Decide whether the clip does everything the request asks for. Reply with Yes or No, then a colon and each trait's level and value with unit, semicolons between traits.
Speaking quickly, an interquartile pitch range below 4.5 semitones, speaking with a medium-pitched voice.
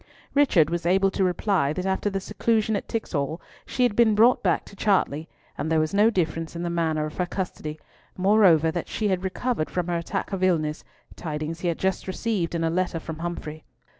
Yes: fast, 210 wpm; average, 3.5 semitones; medium, 180 Hz